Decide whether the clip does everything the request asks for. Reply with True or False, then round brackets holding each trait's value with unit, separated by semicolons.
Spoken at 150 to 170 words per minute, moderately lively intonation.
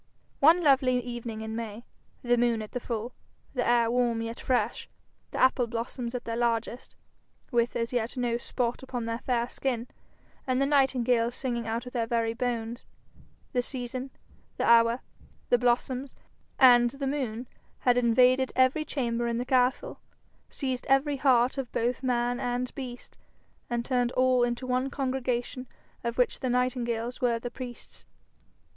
False (160 wpm; 1.5 semitones)